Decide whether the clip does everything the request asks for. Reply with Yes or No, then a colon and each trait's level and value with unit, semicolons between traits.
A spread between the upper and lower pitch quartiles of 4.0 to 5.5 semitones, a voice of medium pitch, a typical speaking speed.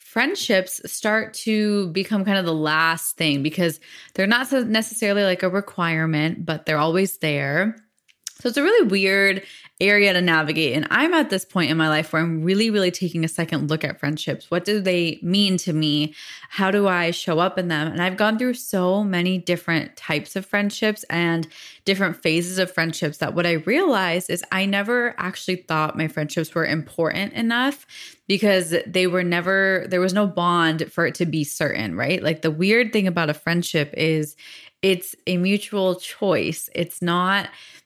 No: average, 3.6 semitones; medium, 180 Hz; average, 185 wpm